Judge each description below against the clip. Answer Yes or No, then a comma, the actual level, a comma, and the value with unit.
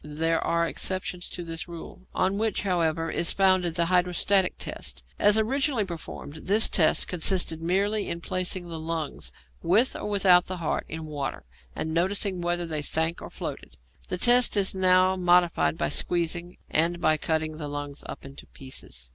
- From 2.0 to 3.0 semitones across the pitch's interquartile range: Yes, average, 2.7 semitones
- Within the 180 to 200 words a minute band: No, average, 170 wpm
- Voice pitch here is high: No, medium, 175 Hz